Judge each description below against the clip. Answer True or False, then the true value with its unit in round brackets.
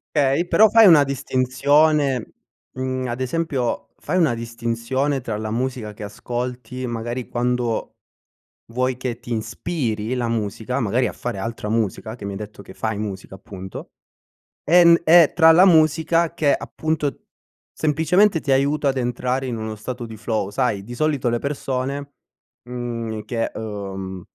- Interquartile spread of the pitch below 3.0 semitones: False (4.1 semitones)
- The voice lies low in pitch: True (125 Hz)